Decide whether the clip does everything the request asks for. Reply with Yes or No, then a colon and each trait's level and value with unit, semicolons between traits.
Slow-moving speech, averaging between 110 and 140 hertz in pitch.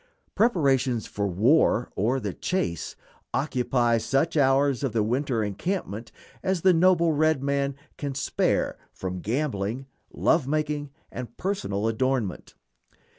Yes: slow, 125 wpm; low, 135 Hz